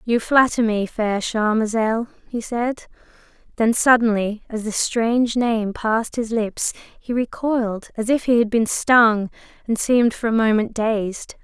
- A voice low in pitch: No, high, 225 Hz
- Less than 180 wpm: Yes, average, 155 wpm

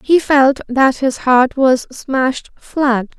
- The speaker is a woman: Yes, female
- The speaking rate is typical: Yes, average, 150 wpm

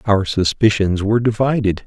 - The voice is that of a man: Yes, male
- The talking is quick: No, slow, 130 wpm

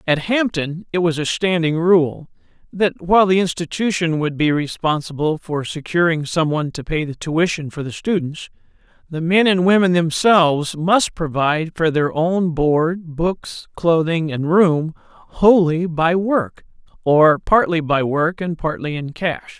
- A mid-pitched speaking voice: Yes, medium, 165 Hz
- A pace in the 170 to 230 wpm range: No, average, 155 wpm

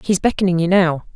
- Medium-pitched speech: Yes, medium, 180 Hz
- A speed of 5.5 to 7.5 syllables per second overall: Yes, 6.0 syllables/s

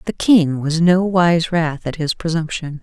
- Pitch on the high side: No, medium, 165 Hz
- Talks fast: No, average, 190 wpm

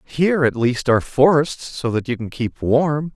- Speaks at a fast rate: Yes, fast, 210 wpm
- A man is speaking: Yes, male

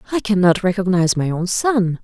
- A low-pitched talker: No, high, 190 Hz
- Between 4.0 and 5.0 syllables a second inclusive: No, 5.6 syllables/s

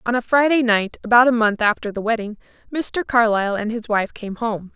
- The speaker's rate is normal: No, fast, 215 wpm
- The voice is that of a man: No, female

